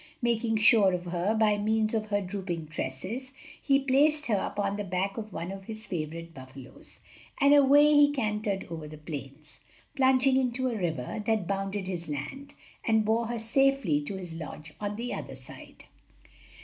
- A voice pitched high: Yes, high, 205 Hz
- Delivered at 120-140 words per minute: No, average, 175 wpm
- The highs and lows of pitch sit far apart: Yes, wide, 5.7 semitones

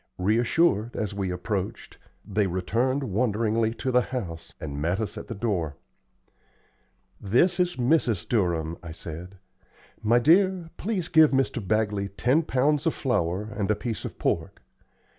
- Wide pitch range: Yes, wide, 5.7 semitones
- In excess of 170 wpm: No, average, 145 wpm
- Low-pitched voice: Yes, low, 110 Hz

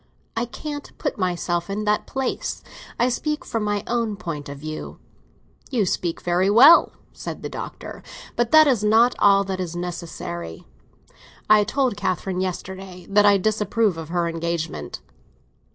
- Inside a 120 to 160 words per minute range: Yes, average, 150 wpm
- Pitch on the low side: No, high, 195 Hz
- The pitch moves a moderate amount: Yes, average, 4.5 semitones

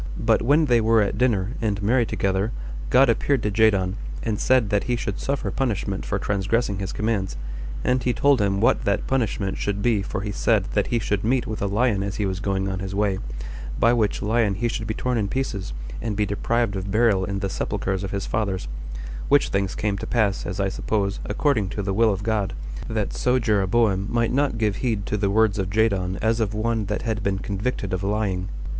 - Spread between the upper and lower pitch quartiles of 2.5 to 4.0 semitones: Yes, average, 2.8 semitones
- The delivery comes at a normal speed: No, fast, 215 wpm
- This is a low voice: Yes, low, 105 Hz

